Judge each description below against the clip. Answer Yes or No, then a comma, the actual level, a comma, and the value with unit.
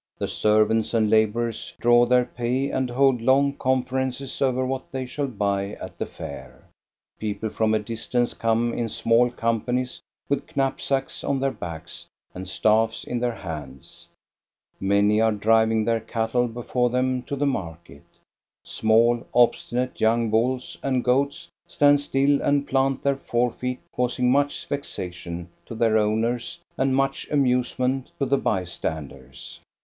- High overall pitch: No, low, 120 Hz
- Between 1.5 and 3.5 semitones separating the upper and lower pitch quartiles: Yes, average, 3.2 semitones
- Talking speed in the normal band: Yes, average, 145 wpm